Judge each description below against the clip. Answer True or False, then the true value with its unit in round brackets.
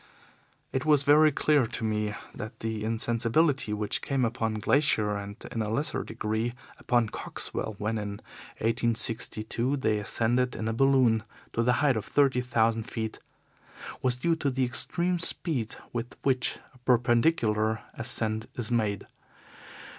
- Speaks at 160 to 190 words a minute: False (145 wpm)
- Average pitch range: True (3.1 semitones)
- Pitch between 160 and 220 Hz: False (115 Hz)